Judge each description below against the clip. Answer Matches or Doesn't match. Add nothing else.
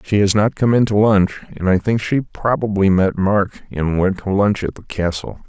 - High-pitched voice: Doesn't match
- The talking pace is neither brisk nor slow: Doesn't match